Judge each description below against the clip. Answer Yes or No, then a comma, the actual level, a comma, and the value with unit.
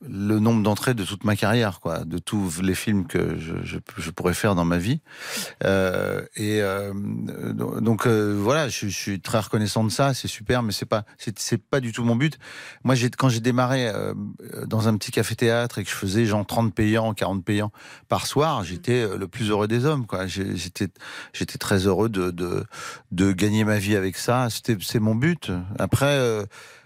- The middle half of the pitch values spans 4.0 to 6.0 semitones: No, average, 3.3 semitones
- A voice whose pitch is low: Yes, low, 110 Hz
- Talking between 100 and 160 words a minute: No, average, 210 wpm